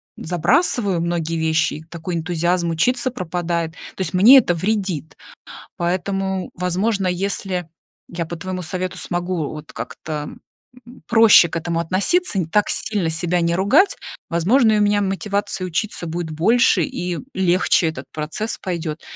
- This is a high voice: No, medium, 180 Hz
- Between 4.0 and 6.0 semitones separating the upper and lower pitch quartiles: No, average, 3.0 semitones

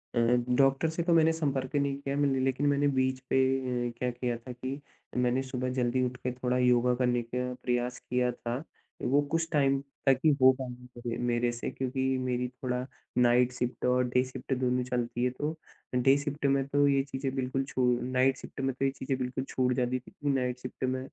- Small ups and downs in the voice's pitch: Yes, narrow, 1.5 semitones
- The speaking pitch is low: Yes, low, 130 Hz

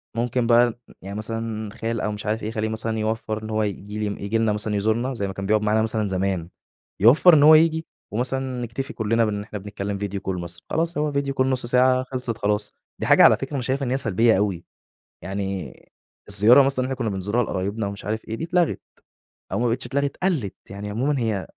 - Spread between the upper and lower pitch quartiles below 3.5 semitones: No, average, 3.8 semitones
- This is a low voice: Yes, low, 110 Hz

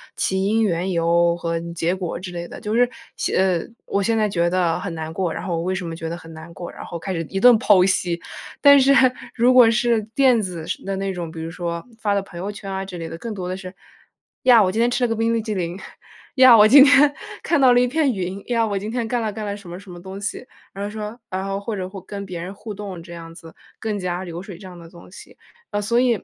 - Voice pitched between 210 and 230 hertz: No, high, 195 Hz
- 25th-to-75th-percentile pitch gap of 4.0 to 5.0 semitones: Yes, average, 4.3 semitones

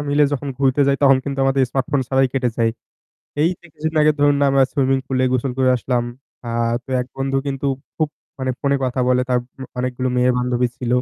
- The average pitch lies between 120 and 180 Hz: Yes, low, 135 Hz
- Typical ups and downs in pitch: No, narrow, 1.6 semitones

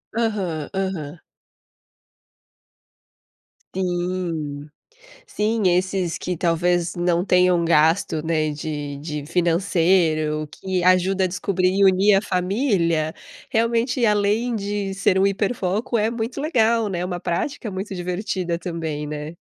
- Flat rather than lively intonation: No, average, 3.3 semitones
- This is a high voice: No, medium, 180 Hz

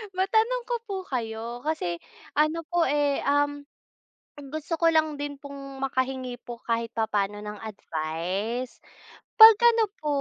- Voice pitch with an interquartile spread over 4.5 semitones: Yes, wide, 5.5 semitones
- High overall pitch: Yes, very high, 275 Hz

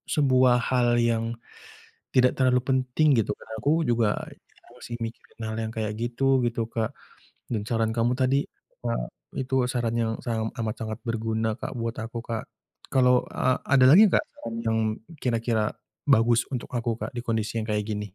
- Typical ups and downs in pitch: No, narrow, 2.1 semitones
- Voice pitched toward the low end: Yes, low, 115 Hz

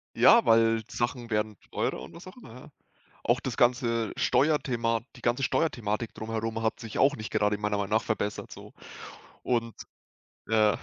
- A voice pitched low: Yes, low, 115 Hz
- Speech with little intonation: Yes, narrow, 2.3 semitones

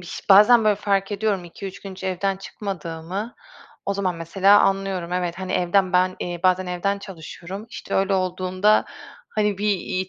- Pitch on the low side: No, high, 190 Hz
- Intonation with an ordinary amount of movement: No, narrow, 1.7 semitones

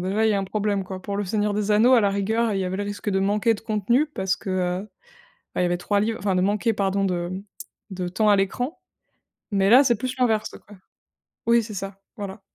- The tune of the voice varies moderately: No, narrow, 2.2 semitones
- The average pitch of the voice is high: Yes, high, 205 Hz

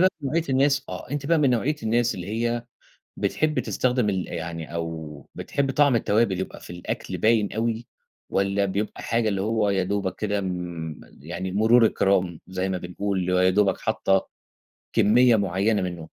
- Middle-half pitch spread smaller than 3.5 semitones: No, average, 4.3 semitones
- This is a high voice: No, low, 100 Hz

